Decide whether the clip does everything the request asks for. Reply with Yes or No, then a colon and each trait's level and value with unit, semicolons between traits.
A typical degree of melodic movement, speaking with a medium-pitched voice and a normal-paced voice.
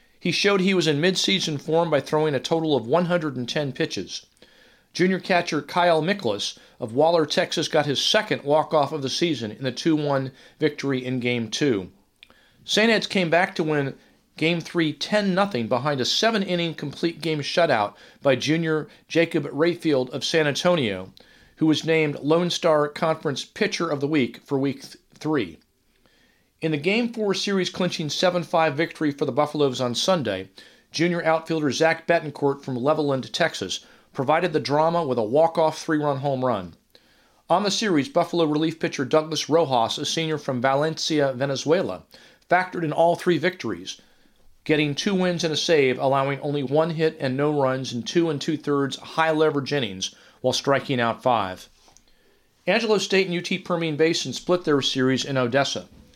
Yes: average, 3.5 semitones; medium, 155 Hz; average, 165 wpm